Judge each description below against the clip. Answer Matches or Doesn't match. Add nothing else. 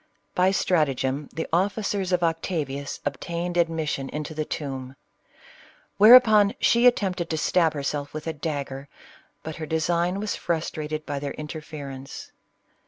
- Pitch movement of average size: Matches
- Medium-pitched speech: Matches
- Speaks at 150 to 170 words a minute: Doesn't match